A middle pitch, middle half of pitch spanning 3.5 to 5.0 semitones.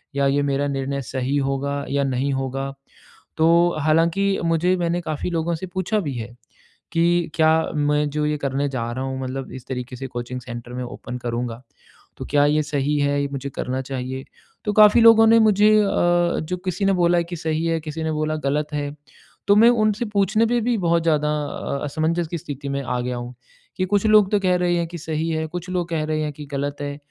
Yes: medium, 155 Hz; average, 4.2 semitones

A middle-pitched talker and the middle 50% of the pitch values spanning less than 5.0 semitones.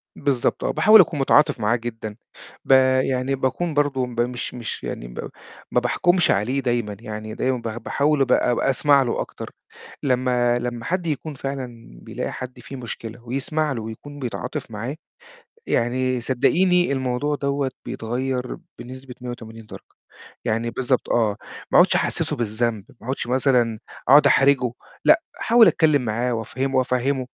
No: low, 125 Hz; average, 2.7 semitones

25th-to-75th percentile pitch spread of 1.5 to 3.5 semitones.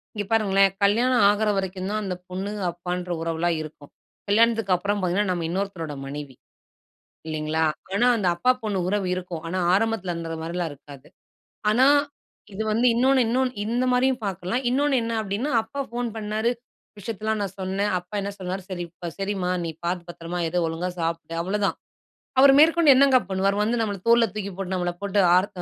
No: average, 4.0 semitones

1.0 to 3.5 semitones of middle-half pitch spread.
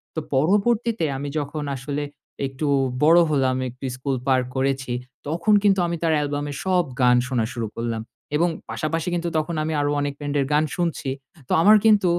No: average, 4.3 semitones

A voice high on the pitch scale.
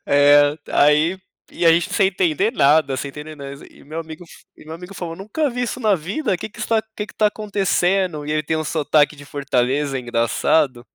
No: medium, 155 Hz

